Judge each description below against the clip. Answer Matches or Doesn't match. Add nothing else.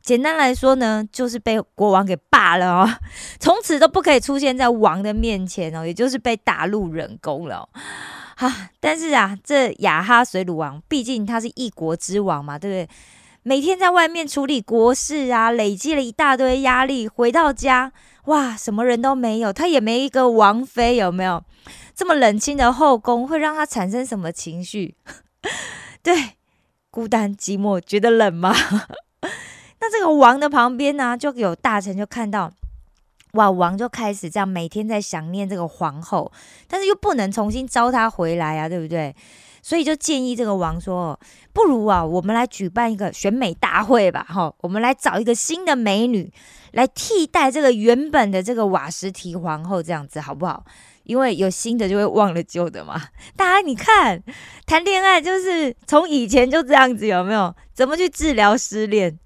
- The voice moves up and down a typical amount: Doesn't match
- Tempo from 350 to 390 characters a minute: Doesn't match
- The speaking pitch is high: Matches